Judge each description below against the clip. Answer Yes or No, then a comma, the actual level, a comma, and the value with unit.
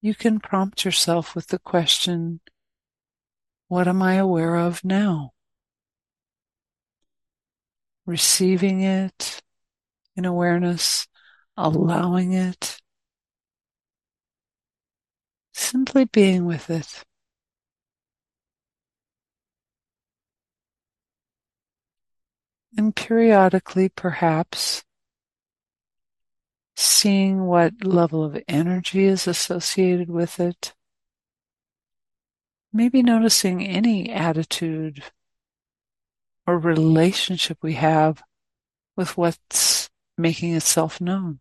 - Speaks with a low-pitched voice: No, medium, 175 Hz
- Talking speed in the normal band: No, slow, 70 wpm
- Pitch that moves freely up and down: No, narrow, 2.5 semitones